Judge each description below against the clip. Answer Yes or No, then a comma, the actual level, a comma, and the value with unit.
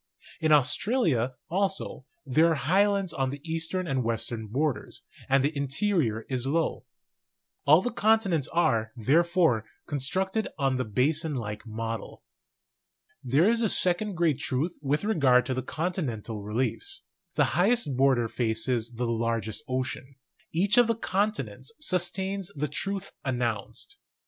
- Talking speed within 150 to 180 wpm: No, average, 140 wpm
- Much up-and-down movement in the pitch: Yes, wide, 6.8 semitones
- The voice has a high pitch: No, medium, 145 Hz